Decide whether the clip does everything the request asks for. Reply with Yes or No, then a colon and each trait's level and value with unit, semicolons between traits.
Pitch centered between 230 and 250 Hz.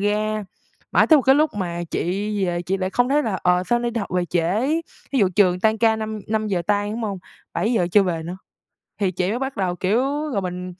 No: high, 205 Hz